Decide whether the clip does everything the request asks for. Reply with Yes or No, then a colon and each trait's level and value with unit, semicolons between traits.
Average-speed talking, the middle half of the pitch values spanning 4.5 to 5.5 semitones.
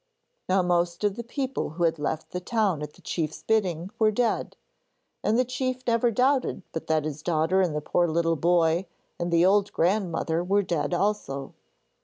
Yes: average, 185 wpm; average, 4.8 semitones